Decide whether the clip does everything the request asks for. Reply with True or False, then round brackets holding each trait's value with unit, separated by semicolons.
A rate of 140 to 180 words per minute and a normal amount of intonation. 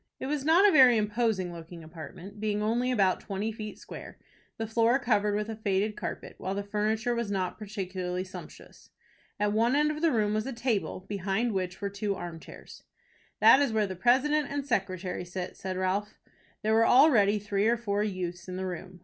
False (200 wpm; 3.8 semitones)